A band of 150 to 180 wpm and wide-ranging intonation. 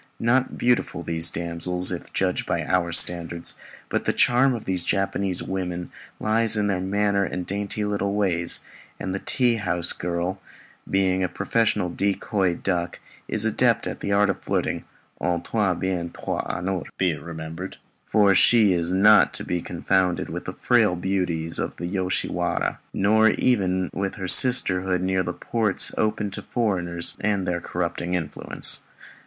No: average, 160 wpm; average, 2.7 semitones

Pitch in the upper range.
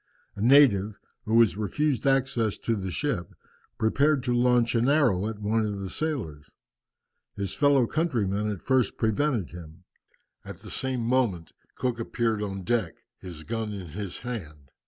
No: low, 110 Hz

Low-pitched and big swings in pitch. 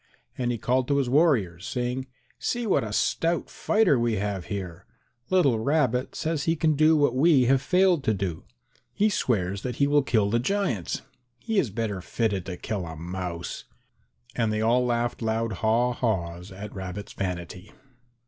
Yes: low, 115 Hz; wide, 6.3 semitones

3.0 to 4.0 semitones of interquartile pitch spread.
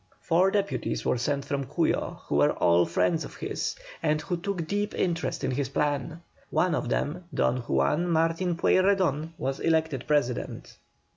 No: average, 4.4 semitones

